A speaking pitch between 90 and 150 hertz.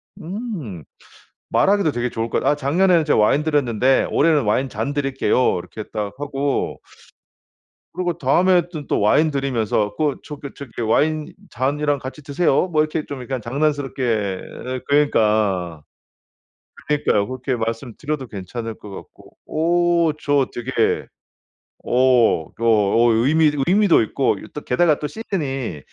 Yes: low, 135 Hz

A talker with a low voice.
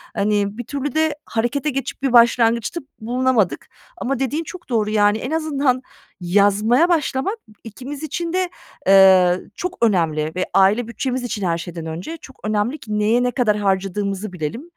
No: high, 230 Hz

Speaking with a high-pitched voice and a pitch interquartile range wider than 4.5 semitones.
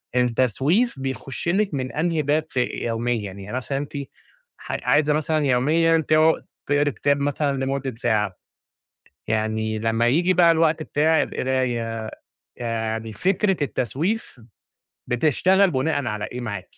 No: low, 135 Hz; average, 5.2 semitones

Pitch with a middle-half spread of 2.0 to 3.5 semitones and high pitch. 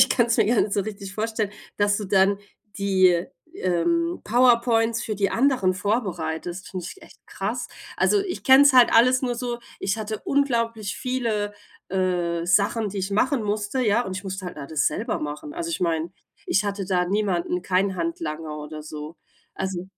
No: average, 4.4 semitones; high, 205 Hz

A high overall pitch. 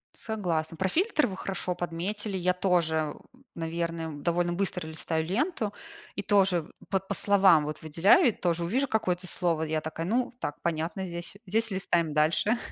No: medium, 180 Hz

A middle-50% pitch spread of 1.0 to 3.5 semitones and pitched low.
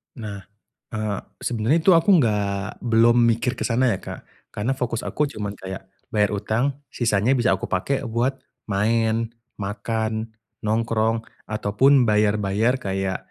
Yes: narrow, 2.5 semitones; low, 110 Hz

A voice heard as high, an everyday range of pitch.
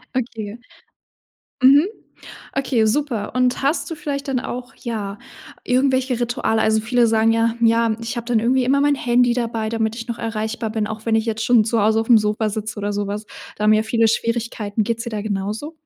No: high, 230 Hz; narrow, 2.2 semitones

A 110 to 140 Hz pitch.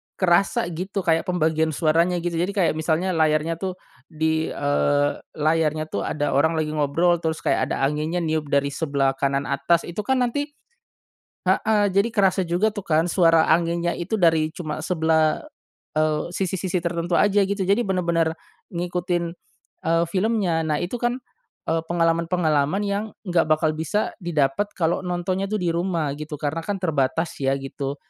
No: medium, 165 Hz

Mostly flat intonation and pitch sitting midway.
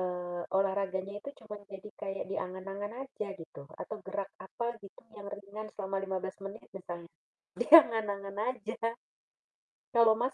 No: narrow, 2.0 semitones; high, 195 Hz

